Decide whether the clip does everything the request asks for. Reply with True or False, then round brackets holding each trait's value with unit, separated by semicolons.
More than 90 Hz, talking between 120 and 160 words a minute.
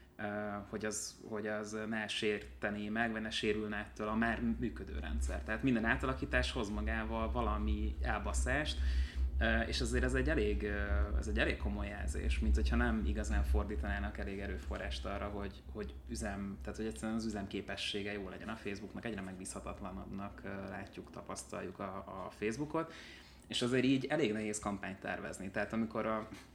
True (100 Hz; 155 wpm)